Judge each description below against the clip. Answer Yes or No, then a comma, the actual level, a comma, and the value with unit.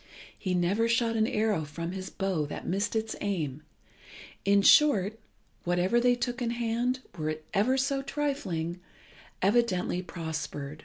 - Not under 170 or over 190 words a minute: No, average, 145 wpm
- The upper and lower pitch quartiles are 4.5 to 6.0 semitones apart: Yes, wide, 5.4 semitones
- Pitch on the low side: No, high, 200 Hz